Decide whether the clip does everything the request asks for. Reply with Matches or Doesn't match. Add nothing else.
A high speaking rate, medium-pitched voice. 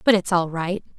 Matches